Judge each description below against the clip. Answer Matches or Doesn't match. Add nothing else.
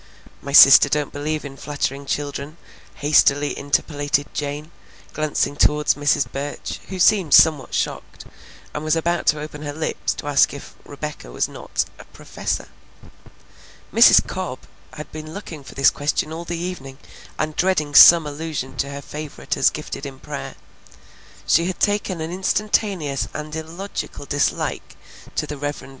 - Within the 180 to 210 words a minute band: Doesn't match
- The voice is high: Doesn't match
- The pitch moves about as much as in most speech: Doesn't match